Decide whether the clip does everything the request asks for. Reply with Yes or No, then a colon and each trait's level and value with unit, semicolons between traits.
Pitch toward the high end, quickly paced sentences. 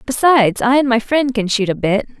Yes: high, 240 Hz; fast, 245 wpm